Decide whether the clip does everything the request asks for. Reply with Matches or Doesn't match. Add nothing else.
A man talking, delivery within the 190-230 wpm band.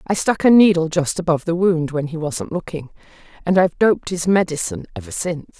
Doesn't match